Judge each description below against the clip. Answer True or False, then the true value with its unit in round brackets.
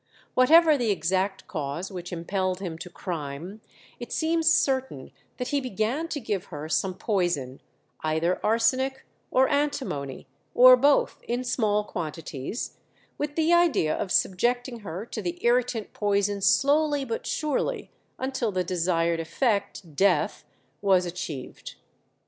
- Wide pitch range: True (6.9 semitones)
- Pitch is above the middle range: True (205 Hz)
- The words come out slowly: True (130 wpm)